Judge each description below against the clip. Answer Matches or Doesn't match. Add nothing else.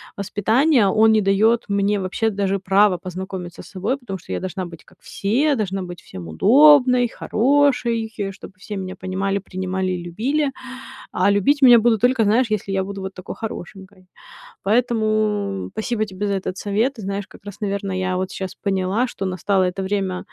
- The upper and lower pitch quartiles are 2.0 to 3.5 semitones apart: Matches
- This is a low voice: Doesn't match